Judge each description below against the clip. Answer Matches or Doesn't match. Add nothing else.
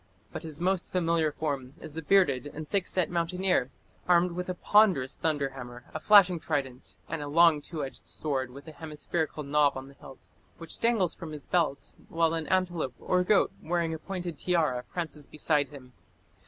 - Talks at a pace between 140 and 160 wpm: Doesn't match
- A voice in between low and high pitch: Matches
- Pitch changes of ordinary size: Matches